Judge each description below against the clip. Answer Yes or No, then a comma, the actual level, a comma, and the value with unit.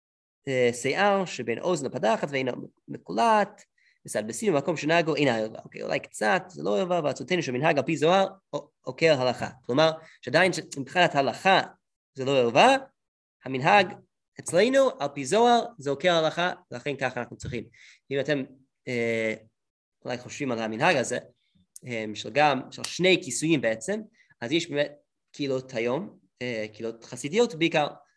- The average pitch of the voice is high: No, medium, 145 Hz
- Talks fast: No, average, 135 wpm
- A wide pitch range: Yes, wide, 6.3 semitones